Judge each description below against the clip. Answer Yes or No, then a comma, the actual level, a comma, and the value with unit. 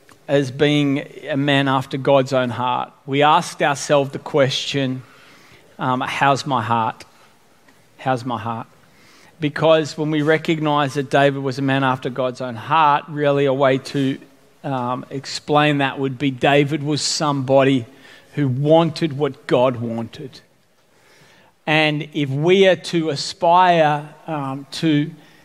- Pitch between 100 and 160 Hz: Yes, medium, 140 Hz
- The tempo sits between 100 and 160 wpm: Yes, slow, 135 wpm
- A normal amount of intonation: No, narrow, 2.2 semitones